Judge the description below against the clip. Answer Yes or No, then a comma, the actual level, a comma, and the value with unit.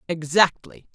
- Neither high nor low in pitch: Yes, medium, 170 Hz